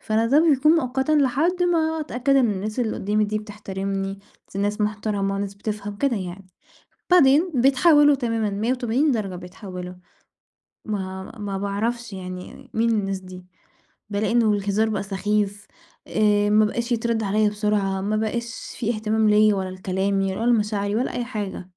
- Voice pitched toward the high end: Yes, high, 210 Hz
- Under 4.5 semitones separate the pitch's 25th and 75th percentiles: Yes, average, 3.2 semitones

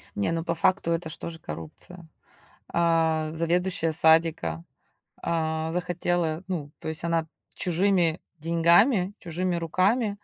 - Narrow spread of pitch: Yes, narrow, 1.8 semitones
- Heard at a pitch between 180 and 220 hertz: No, medium, 165 Hz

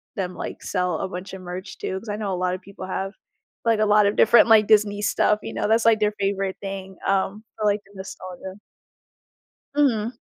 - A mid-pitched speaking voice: No, high, 200 Hz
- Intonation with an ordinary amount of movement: No, narrow, 2.0 semitones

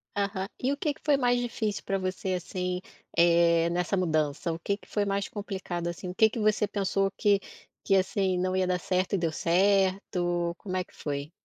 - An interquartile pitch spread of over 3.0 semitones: No, narrow, 2.5 semitones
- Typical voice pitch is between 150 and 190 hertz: Yes, medium, 185 Hz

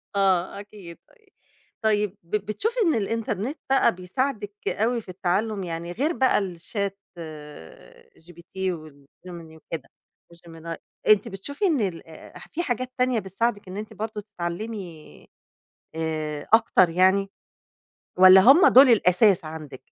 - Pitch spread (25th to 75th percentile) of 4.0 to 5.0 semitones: Yes, average, 4.7 semitones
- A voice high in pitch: Yes, high, 195 Hz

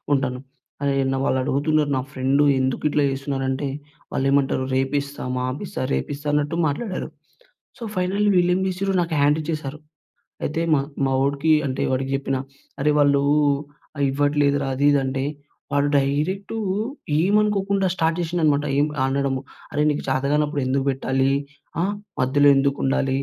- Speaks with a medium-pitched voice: Yes, medium, 145 Hz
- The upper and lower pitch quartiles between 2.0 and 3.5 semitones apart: Yes, narrow, 2.5 semitones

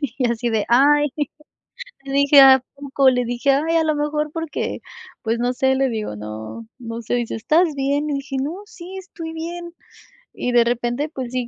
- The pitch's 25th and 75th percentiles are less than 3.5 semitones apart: No, average, 3.8 semitones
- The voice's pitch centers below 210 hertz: No, very high, 270 Hz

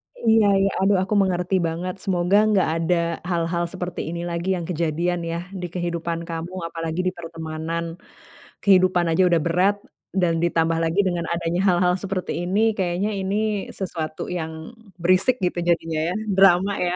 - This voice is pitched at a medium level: Yes, medium, 175 Hz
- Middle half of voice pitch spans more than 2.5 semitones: No, narrow, 2.1 semitones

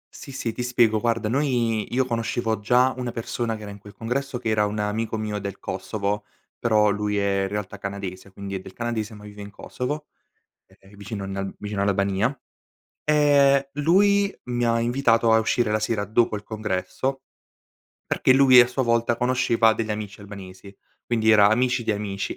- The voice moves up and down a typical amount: Yes, average, 3.1 semitones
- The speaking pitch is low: Yes, low, 110 Hz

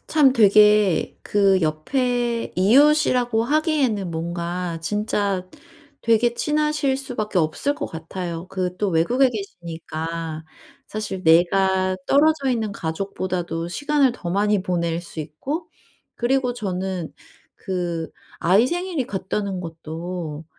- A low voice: No, high, 195 Hz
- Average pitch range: No, wide, 6.2 semitones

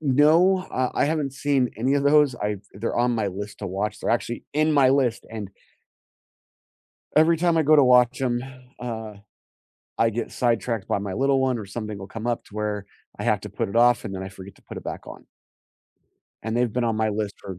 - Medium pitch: No, low, 120 Hz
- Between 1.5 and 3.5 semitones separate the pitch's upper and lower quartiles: No, average, 4.4 semitones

